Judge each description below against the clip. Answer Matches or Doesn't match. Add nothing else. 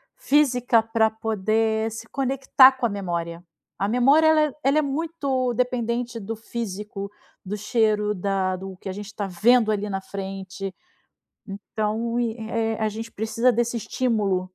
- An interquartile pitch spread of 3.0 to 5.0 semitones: Matches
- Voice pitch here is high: Matches